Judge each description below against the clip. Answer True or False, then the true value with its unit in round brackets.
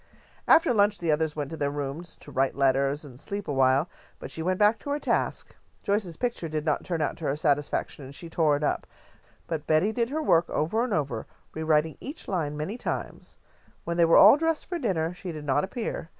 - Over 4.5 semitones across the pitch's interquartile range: True (5.6 semitones)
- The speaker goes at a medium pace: False (220 wpm)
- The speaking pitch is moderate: True (160 Hz)